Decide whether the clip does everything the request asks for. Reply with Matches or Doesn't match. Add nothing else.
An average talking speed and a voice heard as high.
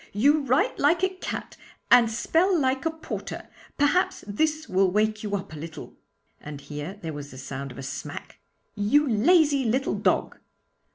Matches